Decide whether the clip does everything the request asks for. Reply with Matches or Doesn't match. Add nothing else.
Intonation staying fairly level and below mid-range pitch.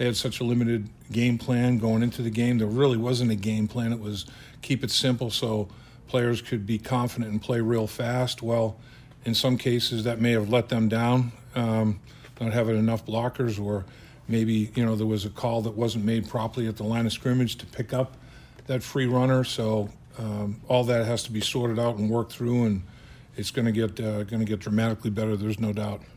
Matches